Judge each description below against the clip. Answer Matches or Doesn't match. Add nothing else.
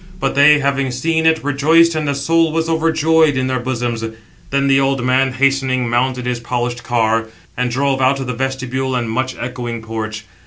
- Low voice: Matches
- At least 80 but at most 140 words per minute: Doesn't match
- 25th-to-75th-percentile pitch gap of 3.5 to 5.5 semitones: Doesn't match